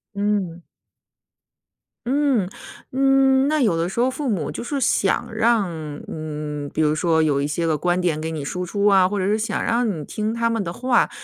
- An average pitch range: No, wide, 6.6 semitones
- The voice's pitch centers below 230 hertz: Yes, high, 195 Hz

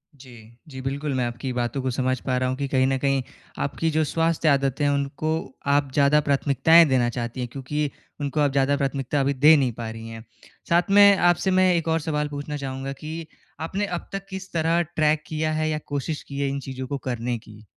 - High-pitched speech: No, medium, 140 Hz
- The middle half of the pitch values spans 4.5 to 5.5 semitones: No, average, 3.1 semitones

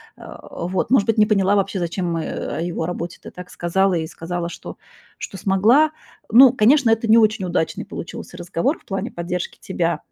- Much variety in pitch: No, average, 3.9 semitones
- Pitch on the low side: No, high, 190 Hz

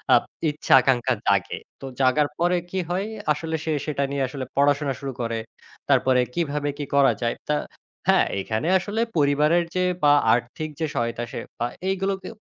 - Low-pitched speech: No, medium, 145 Hz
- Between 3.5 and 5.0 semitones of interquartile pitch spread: Yes, average, 3.8 semitones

